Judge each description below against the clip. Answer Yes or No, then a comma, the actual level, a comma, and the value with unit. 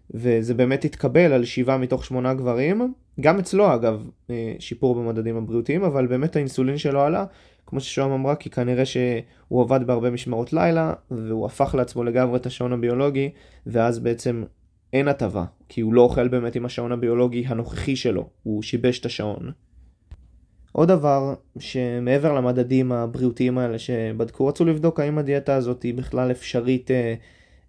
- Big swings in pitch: No, narrow, 2.6 semitones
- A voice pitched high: No, low, 125 Hz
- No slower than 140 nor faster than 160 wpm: Yes, fast, 150 wpm